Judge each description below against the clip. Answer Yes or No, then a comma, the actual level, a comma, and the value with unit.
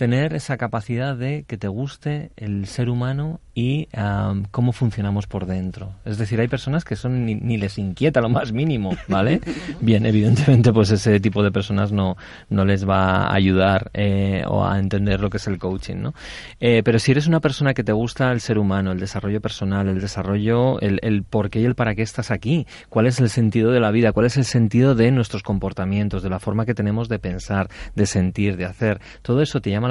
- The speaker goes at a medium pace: No, fast, 220 wpm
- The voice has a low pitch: Yes, low, 110 Hz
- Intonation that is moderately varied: Yes, average, 3.8 semitones